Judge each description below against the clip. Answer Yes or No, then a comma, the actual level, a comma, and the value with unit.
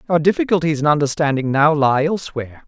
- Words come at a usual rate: Yes, average, 155 wpm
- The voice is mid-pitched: Yes, medium, 150 Hz